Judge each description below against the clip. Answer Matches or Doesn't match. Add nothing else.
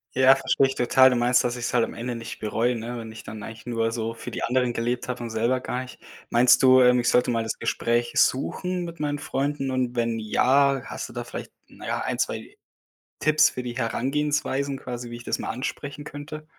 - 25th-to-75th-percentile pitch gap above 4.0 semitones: Doesn't match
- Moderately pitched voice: Doesn't match